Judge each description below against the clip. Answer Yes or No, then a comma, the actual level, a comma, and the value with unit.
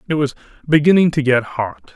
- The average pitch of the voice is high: No, medium, 140 Hz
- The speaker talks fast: No, average, 185 wpm